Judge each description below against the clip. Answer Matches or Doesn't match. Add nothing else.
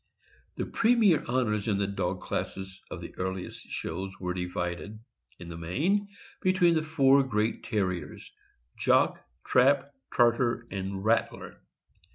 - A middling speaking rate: Doesn't match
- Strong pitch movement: Matches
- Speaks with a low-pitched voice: Matches